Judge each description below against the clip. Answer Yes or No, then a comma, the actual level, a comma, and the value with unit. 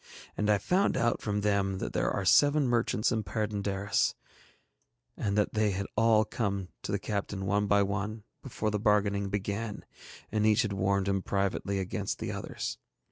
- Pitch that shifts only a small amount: Yes, narrow, 1.5 semitones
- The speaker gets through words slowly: No, average, 175 wpm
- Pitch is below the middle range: Yes, low, 105 Hz